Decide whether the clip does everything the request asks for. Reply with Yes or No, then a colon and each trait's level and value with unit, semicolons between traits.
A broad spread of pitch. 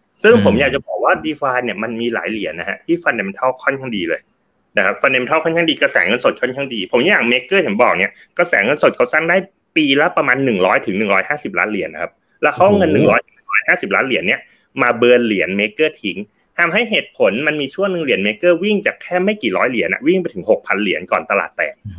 Yes: wide, 8.3 semitones